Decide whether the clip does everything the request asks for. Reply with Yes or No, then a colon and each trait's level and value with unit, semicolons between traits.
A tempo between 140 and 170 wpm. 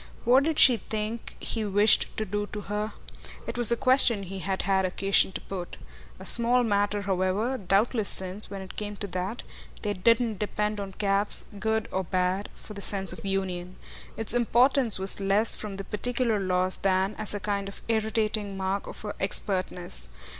No: average, 180 wpm